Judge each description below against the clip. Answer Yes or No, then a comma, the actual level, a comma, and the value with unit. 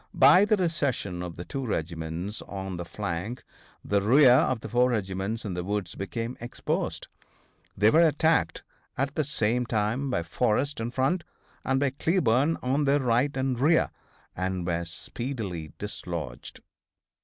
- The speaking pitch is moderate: No, low, 115 Hz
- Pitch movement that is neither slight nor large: No, wide, 6.3 semitones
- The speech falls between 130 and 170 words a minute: Yes, average, 155 wpm